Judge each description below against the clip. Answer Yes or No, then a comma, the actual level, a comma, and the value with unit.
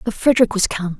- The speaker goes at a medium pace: No, fast, 240 wpm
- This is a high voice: Yes, high, 210 Hz